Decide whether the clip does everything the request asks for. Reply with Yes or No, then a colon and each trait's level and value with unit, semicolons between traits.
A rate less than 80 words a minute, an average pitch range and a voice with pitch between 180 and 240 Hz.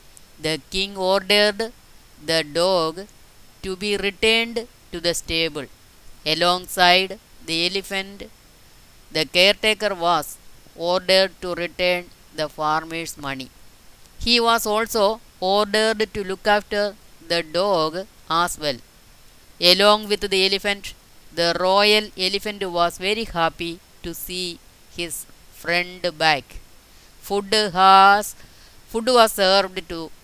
No: average, 110 wpm; average, 3.8 semitones; medium, 185 Hz